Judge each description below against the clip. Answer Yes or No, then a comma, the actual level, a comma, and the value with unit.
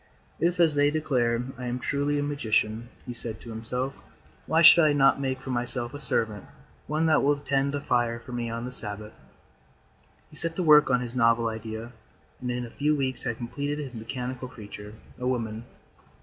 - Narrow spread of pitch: No, average, 3.6 semitones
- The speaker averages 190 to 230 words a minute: Yes, average, 200 wpm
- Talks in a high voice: No, low, 125 Hz